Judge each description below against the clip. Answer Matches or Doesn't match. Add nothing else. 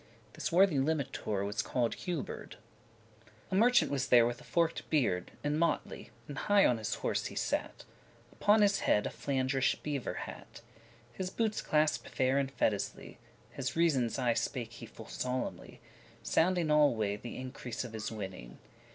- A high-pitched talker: Doesn't match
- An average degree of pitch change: Doesn't match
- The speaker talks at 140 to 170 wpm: Matches